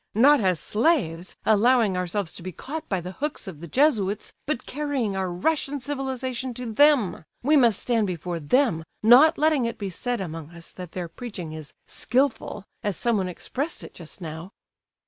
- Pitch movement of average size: No, wide, 6.7 semitones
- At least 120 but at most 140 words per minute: No, average, 175 wpm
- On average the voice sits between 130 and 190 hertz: No, high, 220 Hz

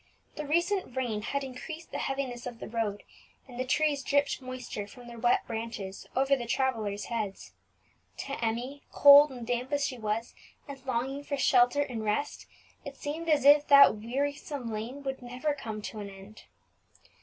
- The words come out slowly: No, average, 175 wpm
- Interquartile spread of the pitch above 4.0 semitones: No, average, 3.7 semitones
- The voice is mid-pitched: No, very high, 255 Hz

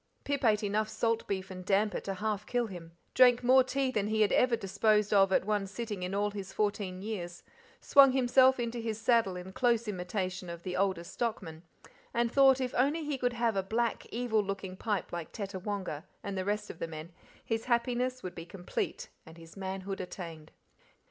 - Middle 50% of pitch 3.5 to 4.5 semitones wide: Yes, average, 4.0 semitones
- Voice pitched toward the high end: Yes, high, 205 Hz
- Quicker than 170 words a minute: Yes, average, 195 wpm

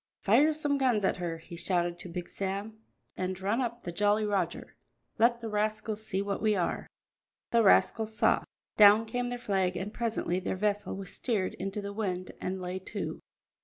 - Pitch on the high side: Yes, high, 205 Hz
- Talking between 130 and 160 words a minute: No, average, 185 wpm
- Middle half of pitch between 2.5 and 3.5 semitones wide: Yes, average, 3.0 semitones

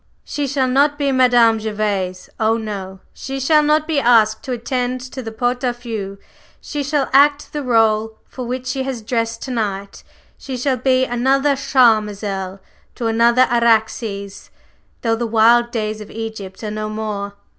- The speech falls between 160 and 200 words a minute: Yes, average, 165 wpm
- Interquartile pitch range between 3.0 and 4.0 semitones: Yes, average, 3.3 semitones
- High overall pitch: Yes, high, 235 Hz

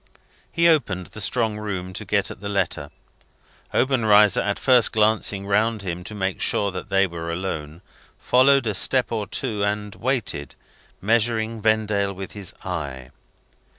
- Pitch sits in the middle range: No, low, 105 Hz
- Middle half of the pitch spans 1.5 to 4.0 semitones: Yes, average, 2.8 semitones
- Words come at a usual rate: Yes, average, 150 wpm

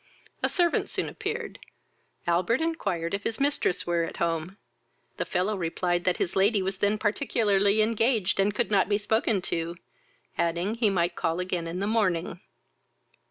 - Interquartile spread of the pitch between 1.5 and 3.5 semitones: No, average, 3.9 semitones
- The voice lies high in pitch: Yes, high, 195 Hz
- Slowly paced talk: No, average, 160 wpm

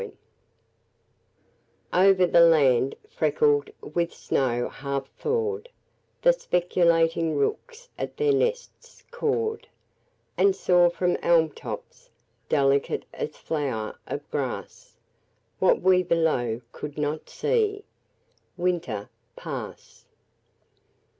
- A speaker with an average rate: No, slow, 95 wpm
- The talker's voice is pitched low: No, medium, 175 Hz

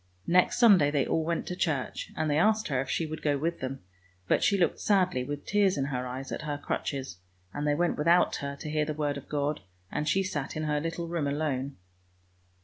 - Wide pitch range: No, average, 3.2 semitones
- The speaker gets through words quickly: Yes, fast, 230 wpm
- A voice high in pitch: No, medium, 150 Hz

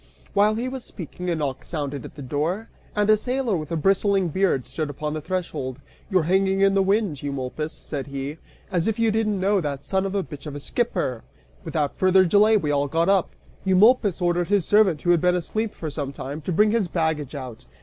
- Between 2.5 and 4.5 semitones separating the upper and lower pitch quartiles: No, average, 5.3 semitones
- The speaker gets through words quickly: Yes, fast, 220 wpm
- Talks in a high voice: No, medium, 175 Hz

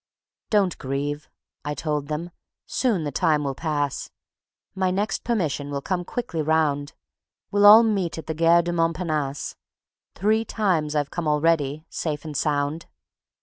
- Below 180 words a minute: Yes, average, 145 wpm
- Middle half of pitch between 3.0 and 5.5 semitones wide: Yes, average, 3.8 semitones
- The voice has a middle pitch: Yes, medium, 160 Hz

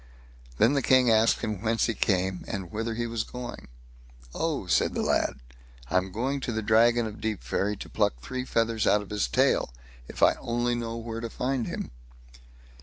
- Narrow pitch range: Yes, narrow, 2.3 semitones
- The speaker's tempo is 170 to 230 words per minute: Yes, average, 185 wpm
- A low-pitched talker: Yes, low, 115 Hz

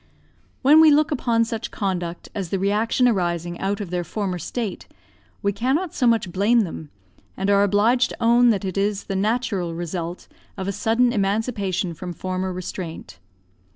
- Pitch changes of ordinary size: Yes, average, 4.0 semitones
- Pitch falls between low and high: No, high, 200 Hz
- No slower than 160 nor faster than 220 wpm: Yes, average, 170 wpm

